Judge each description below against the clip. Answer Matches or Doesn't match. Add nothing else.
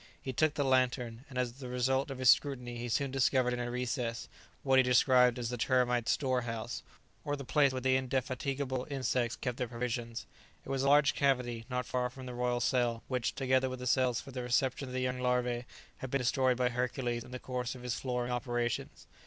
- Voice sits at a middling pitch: Doesn't match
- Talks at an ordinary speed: Doesn't match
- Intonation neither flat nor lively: Doesn't match